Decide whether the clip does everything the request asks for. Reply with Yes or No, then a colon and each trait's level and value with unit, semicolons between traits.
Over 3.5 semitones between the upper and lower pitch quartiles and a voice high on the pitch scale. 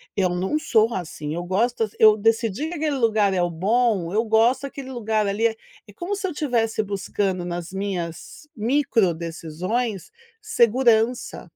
Yes: average, 4.6 semitones; high, 220 Hz